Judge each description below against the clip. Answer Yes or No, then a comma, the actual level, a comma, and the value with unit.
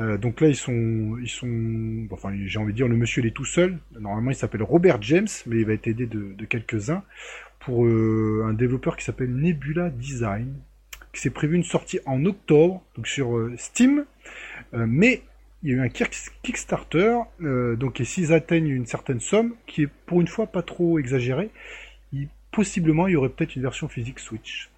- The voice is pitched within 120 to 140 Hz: Yes, low, 135 Hz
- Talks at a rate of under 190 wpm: No, average, 200 wpm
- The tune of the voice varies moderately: No, wide, 6.6 semitones